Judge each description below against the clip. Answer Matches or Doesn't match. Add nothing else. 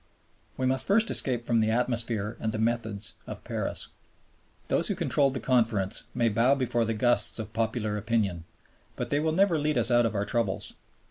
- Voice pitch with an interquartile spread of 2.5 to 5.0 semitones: Matches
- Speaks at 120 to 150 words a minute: Doesn't match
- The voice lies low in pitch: Matches